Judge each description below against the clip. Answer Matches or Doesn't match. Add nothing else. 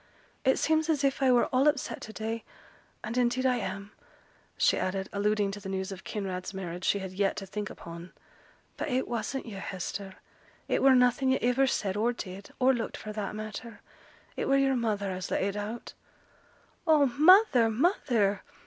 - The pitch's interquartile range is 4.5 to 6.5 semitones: Matches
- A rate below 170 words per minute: Doesn't match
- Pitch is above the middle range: Matches